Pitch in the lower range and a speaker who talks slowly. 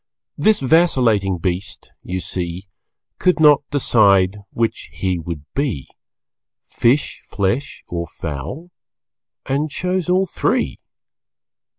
Yes: low, 110 Hz; slow, 100 wpm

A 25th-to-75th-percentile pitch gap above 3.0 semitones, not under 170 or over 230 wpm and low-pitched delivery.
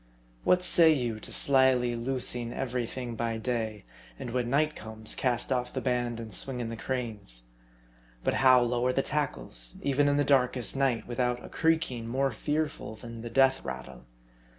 No: narrow, 2.6 semitones; average, 175 wpm; low, 125 Hz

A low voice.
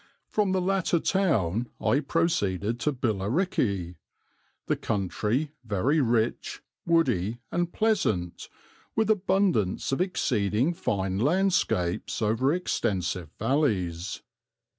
Yes: low, 120 Hz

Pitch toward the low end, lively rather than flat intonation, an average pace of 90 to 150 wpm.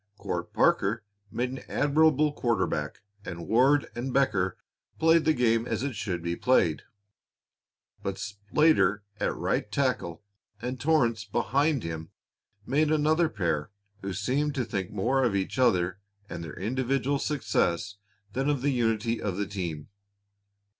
Yes: low, 115 Hz; wide, 6.0 semitones; average, 145 wpm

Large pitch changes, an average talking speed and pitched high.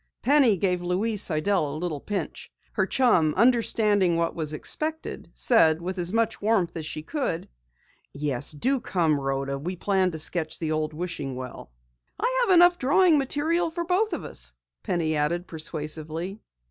No: wide, 7.7 semitones; average, 160 wpm; medium, 180 Hz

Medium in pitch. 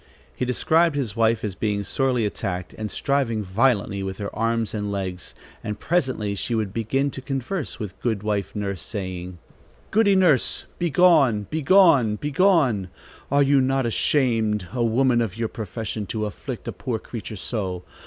No: low, 115 Hz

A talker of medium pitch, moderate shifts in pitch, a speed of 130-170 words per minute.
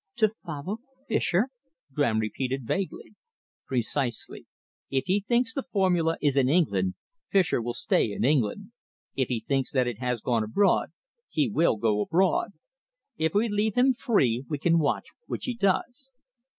No: medium, 155 Hz; wide, 8.7 semitones; average, 155 wpm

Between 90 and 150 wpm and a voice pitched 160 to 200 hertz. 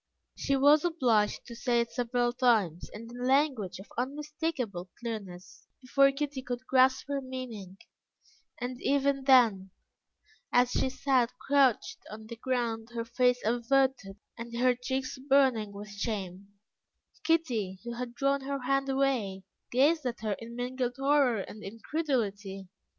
No: average, 140 wpm; high, 245 Hz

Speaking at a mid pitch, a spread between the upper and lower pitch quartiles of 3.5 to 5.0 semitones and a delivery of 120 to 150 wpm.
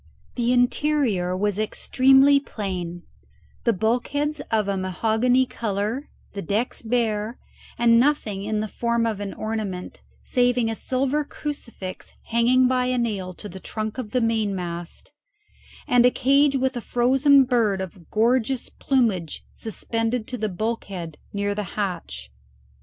No: high, 225 Hz; average, 3.9 semitones; average, 140 wpm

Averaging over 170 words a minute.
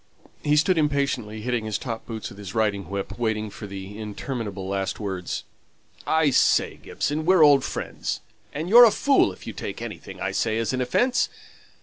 Yes: average, 185 wpm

